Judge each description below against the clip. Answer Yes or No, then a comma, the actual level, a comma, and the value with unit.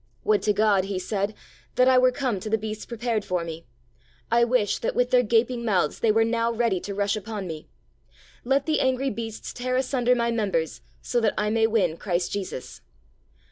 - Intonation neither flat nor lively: Yes, average, 3.2 semitones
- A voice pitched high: Yes, high, 220 Hz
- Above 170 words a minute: Yes, average, 200 wpm